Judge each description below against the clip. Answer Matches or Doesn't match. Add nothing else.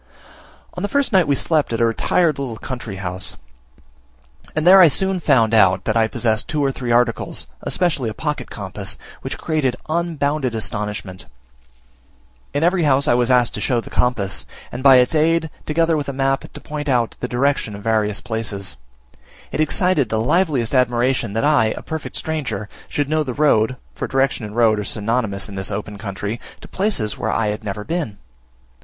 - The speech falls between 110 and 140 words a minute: Doesn't match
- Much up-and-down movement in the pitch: Matches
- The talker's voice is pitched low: Matches